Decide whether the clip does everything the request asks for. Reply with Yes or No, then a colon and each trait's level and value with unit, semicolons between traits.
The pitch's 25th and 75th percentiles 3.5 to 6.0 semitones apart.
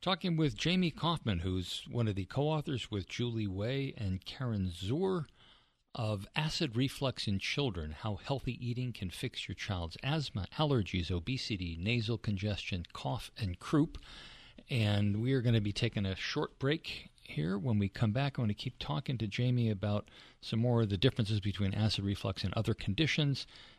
Yes: average, 4.9 semitones